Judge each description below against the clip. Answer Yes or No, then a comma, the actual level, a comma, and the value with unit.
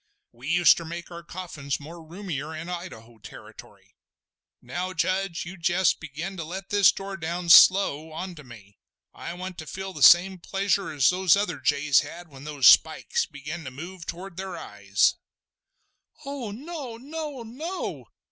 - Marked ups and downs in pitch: No, average, 4.0 semitones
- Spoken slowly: No, average, 160 wpm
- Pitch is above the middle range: No, medium, 175 Hz